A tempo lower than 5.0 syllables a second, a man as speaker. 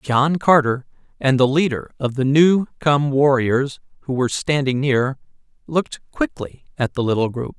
Yes: 4.5 syllables/s; male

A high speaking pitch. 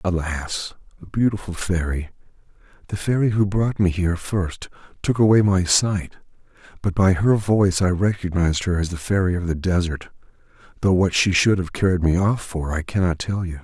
No: very low, 90 Hz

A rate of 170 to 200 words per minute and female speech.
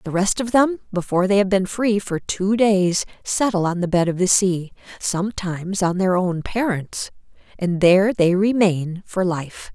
Yes: average, 180 wpm; female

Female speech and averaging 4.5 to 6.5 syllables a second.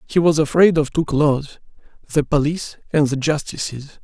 No: male; 5.2 syllables/s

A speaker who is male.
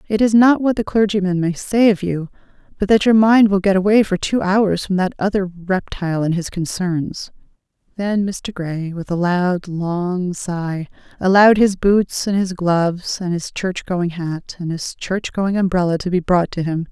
No: female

